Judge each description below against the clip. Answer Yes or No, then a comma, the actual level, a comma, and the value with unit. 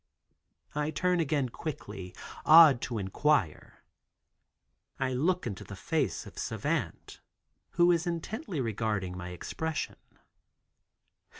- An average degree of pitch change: No, wide, 8.3 semitones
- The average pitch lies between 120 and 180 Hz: Yes, medium, 140 Hz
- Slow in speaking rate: Yes, slow, 105 wpm